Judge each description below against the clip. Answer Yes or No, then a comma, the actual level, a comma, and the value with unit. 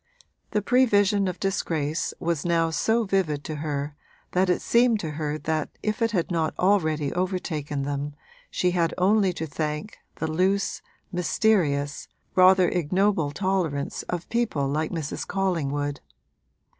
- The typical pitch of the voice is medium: Yes, medium, 170 Hz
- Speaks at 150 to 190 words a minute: No, average, 140 wpm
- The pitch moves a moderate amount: Yes, average, 4.4 semitones